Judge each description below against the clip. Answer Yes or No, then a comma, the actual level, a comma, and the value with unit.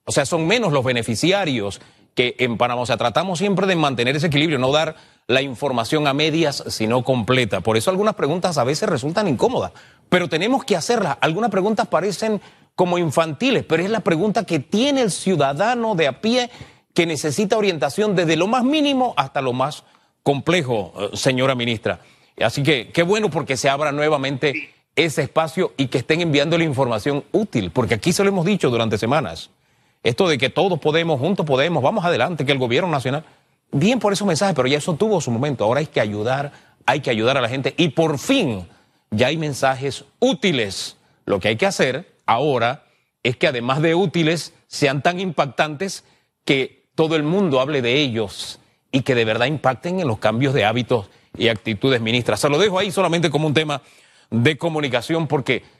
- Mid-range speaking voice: Yes, medium, 150 Hz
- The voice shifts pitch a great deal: Yes, wide, 5.7 semitones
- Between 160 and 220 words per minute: Yes, fast, 190 wpm